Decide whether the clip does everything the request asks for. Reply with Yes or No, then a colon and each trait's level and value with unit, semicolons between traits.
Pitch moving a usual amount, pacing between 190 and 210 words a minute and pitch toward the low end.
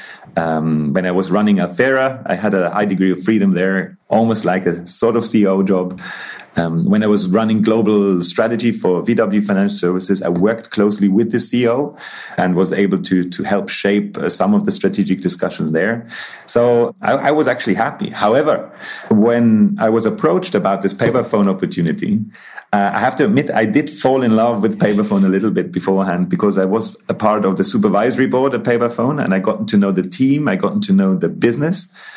Yes: average, 3.9 semitones; average, 200 wpm; low, 105 Hz